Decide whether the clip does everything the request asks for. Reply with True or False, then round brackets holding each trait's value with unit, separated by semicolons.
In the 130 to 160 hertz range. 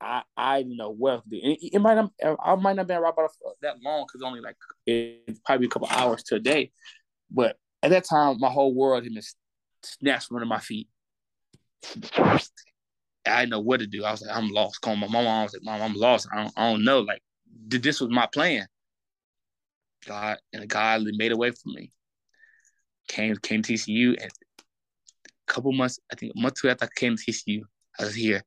False (120 Hz)